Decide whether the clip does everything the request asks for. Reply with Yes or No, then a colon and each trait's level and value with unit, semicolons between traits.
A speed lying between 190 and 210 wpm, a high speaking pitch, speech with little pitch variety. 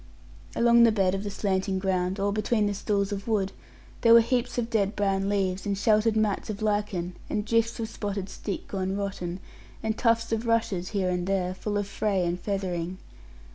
Yes: average, 195 wpm; high, 200 Hz; narrow, 2.3 semitones